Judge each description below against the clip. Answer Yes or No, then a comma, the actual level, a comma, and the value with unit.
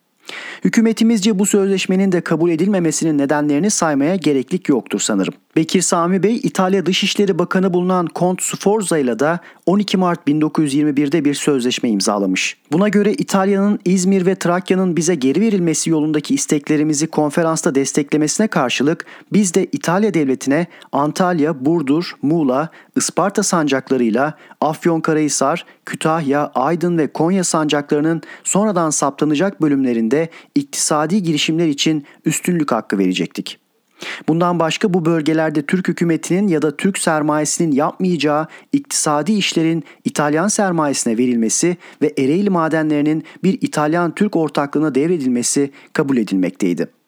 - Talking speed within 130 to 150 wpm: No, average, 120 wpm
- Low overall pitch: No, medium, 165 Hz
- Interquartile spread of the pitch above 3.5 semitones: Yes, average, 3.9 semitones